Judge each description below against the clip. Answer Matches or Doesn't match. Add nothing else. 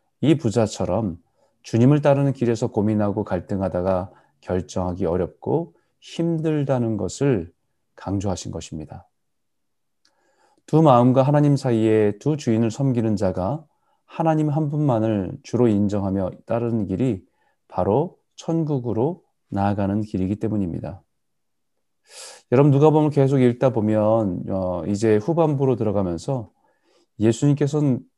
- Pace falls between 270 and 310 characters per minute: Matches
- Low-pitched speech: Matches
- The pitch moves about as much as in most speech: Doesn't match